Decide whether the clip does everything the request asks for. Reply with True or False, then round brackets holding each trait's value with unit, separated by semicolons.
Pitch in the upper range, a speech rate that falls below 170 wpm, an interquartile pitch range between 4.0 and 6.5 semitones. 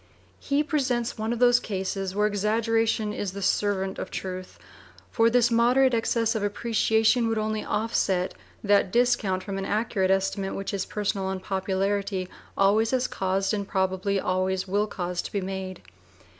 False (205 Hz; 155 wpm; 2.9 semitones)